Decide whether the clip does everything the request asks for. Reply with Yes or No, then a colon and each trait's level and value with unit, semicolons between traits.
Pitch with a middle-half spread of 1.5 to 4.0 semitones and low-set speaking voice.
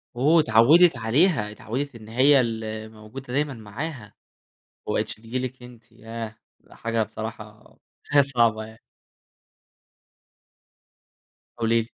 Yes: average, 3.2 semitones; low, 115 Hz